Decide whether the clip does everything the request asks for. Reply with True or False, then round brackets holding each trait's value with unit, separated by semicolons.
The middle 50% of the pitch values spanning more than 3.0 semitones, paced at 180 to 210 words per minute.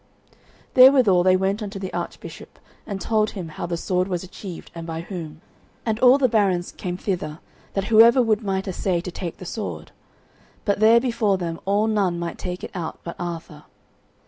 True (3.7 semitones; 185 wpm)